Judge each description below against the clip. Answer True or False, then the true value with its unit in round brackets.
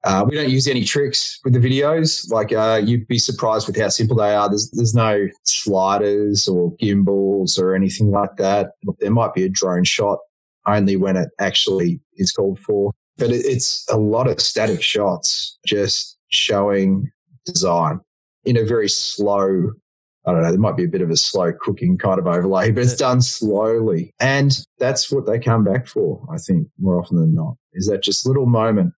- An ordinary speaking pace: True (195 wpm)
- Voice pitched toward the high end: False (110 Hz)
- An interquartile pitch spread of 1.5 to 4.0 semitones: False (5.0 semitones)